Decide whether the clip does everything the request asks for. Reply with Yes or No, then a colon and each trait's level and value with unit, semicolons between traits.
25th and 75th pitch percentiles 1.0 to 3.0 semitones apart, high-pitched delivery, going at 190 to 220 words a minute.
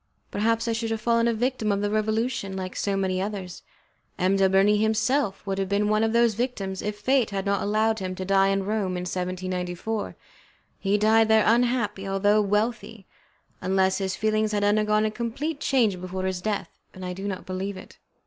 Yes: narrow, 2.4 semitones; high, 205 Hz; average, 195 wpm